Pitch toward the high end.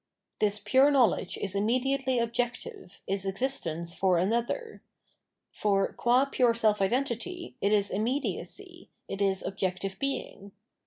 Yes: high, 220 Hz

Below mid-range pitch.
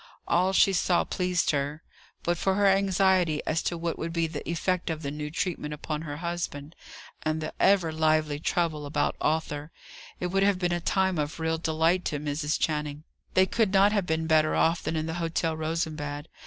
No: medium, 160 Hz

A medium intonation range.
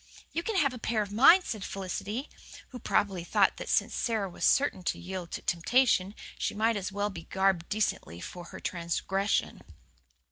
Yes: average, 3.9 semitones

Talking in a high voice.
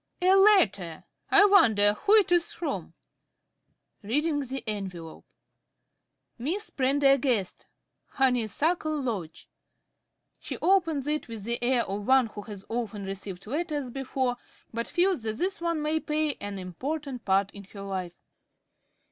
Yes: very high, 255 Hz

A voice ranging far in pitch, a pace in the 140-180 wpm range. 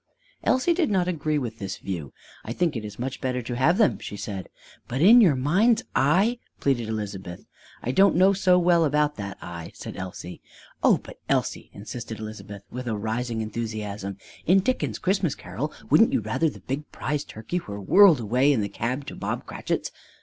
No: wide, 8.6 semitones; average, 195 wpm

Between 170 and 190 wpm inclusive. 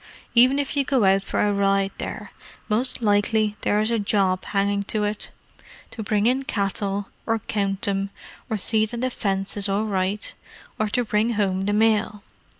Yes: average, 180 wpm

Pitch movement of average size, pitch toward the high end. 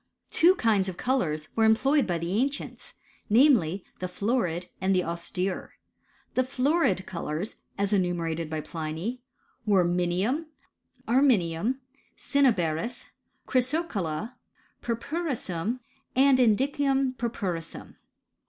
No: wide, 6.8 semitones; high, 205 Hz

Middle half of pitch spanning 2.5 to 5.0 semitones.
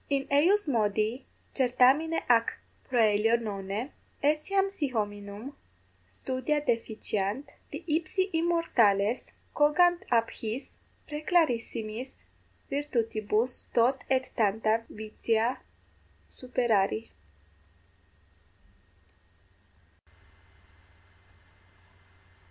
No: wide, 5.4 semitones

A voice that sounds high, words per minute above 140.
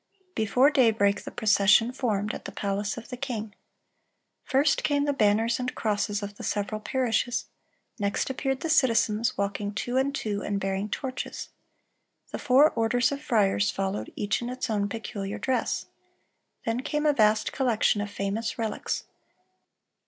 Yes: high, 225 Hz; average, 155 wpm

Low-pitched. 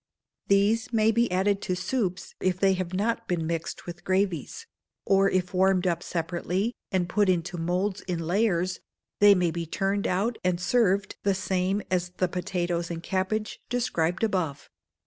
No: medium, 185 Hz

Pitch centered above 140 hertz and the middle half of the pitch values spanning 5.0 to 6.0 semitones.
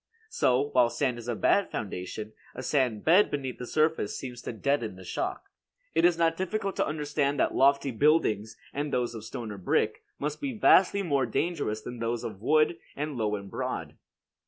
No: low, 135 Hz; wide, 5.4 semitones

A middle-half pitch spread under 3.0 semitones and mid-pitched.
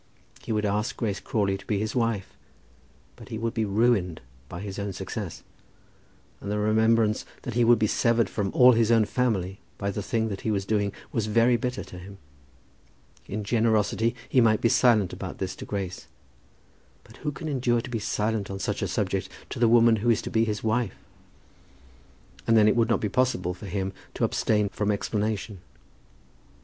No: narrow, 2.5 semitones; low, 110 Hz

